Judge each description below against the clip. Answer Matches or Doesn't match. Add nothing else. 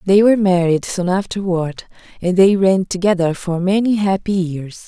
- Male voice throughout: Doesn't match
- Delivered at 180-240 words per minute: Doesn't match